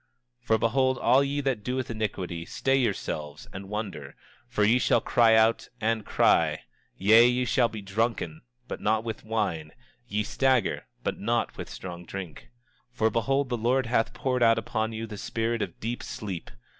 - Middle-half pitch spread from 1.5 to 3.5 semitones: Yes, average, 2.9 semitones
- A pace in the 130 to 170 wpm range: No, average, 180 wpm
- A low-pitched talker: Yes, low, 115 Hz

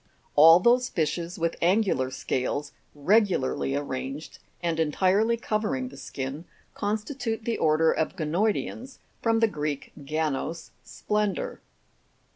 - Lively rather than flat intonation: Yes, wide, 6.3 semitones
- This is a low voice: No, medium, 170 Hz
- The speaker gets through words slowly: Yes, slow, 115 wpm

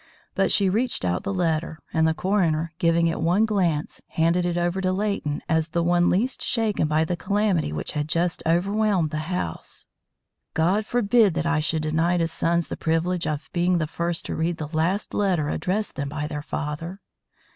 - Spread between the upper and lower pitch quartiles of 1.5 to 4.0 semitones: Yes, average, 3.0 semitones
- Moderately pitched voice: Yes, medium, 170 Hz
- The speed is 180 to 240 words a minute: Yes, average, 190 wpm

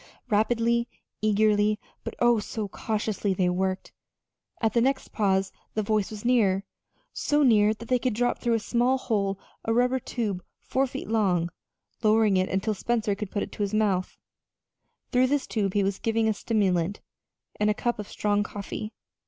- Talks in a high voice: Yes, high, 215 Hz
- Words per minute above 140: Yes, average, 175 wpm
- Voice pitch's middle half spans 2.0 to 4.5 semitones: Yes, average, 2.8 semitones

